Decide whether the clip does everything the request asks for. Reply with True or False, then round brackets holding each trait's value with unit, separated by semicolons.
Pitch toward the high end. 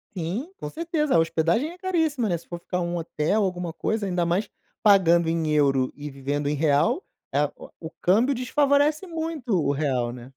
False (180 Hz)